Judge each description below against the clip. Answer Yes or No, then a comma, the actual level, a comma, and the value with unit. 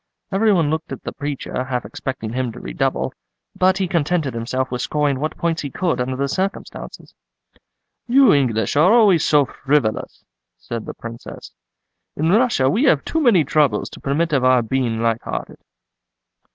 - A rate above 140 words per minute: Yes, average, 170 wpm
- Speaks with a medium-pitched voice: Yes, medium, 145 Hz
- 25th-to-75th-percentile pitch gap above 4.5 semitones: Yes, wide, 5.5 semitones